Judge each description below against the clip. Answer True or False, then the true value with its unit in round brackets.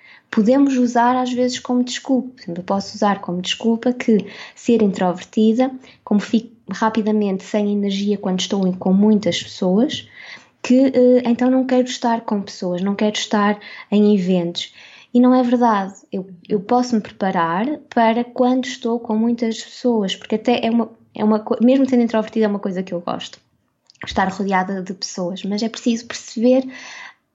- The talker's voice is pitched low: False (225 Hz)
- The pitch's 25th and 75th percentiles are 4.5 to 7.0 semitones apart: False (3.7 semitones)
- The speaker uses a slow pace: False (160 wpm)